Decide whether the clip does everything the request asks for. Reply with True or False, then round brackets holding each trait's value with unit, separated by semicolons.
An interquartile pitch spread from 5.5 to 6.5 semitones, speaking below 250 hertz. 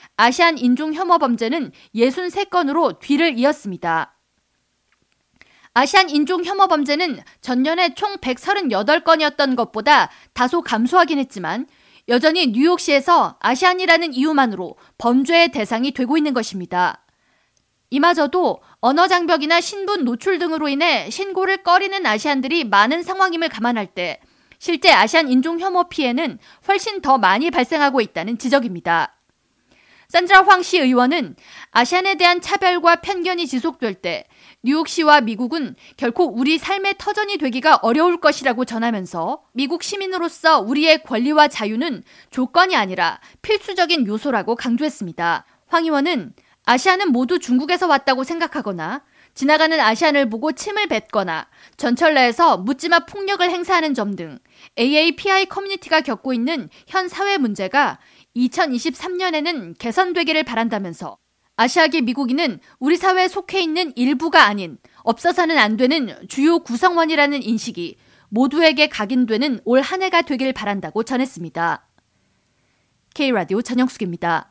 False (6.2 semitones; 295 Hz)